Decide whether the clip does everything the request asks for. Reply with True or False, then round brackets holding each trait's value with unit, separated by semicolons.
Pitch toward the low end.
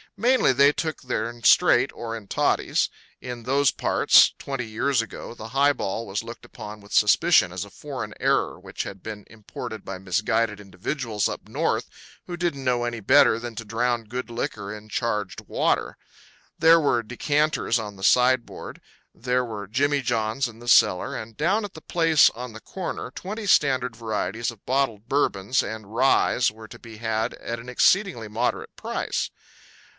True (115 Hz)